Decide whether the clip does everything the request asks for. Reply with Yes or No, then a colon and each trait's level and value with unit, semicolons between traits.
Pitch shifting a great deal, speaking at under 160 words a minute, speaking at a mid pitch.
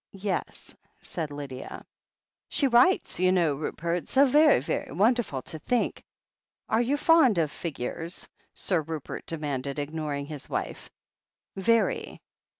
Yes: wide, 8.5 semitones; slow, 135 wpm; medium, 170 Hz